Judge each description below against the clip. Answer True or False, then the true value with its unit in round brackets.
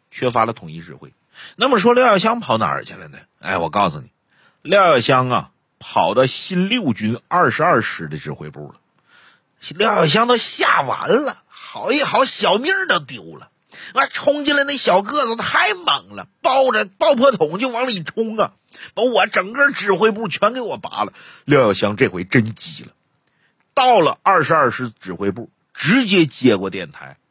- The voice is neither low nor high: False (195 Hz)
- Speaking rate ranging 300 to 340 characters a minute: False (250 characters per minute)